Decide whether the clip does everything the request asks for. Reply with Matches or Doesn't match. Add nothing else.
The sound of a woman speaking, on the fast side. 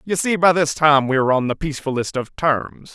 Doesn't match